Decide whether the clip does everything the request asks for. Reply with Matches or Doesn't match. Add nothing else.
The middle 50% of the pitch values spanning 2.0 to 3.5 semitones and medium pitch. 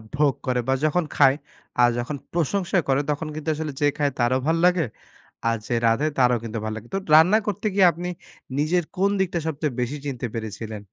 Doesn't match